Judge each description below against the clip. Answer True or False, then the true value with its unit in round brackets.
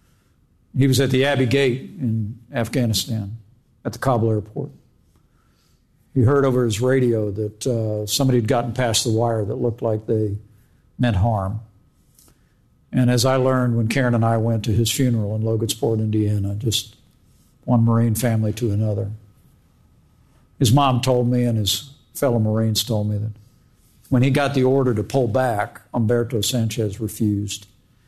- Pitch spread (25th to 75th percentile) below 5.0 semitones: True (2.8 semitones)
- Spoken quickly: False (160 wpm)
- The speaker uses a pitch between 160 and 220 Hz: False (115 Hz)